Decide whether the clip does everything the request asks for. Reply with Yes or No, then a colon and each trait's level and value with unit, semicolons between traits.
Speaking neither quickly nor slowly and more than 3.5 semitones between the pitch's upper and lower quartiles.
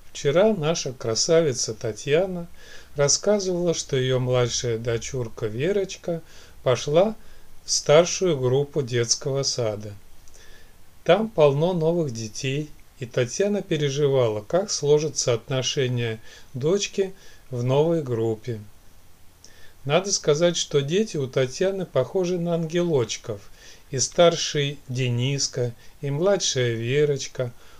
No: slow, 95 wpm; wide, 5.6 semitones